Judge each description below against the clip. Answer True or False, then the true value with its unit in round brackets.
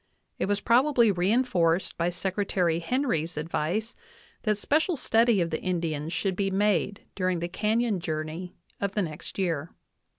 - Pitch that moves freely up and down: False (4.1 semitones)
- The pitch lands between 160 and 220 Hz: True (190 Hz)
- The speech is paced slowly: False (145 wpm)